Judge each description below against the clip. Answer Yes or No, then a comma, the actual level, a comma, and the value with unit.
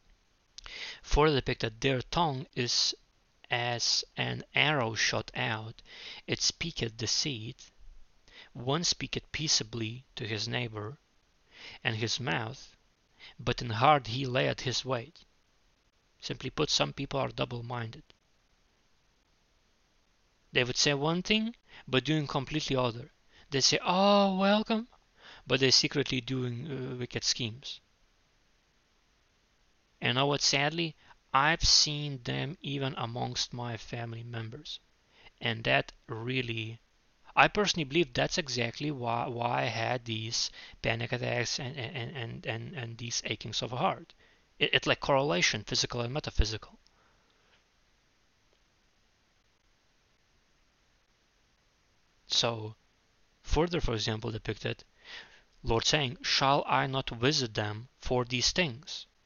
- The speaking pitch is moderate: No, low, 125 Hz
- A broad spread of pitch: No, average, 3.9 semitones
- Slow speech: Yes, slow, 115 wpm